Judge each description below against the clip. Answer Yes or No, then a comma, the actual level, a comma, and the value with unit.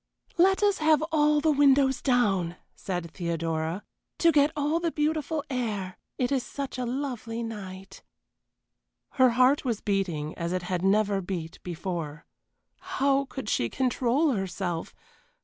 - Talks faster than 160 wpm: No, average, 140 wpm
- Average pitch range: No, wide, 7.5 semitones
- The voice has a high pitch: Yes, high, 235 Hz